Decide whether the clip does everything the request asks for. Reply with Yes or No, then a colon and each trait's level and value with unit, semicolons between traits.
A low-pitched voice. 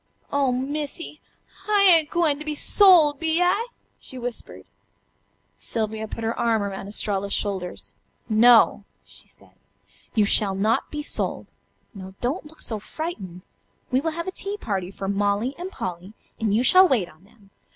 No: high, 235 Hz